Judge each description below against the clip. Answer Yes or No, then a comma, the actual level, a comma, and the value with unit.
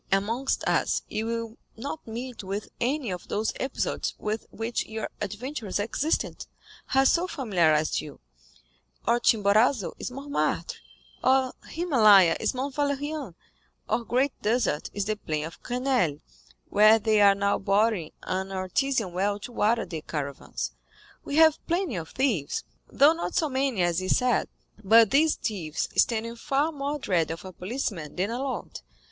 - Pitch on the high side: Yes, high, 225 Hz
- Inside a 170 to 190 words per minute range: No, average, 155 wpm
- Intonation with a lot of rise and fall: Yes, wide, 5.7 semitones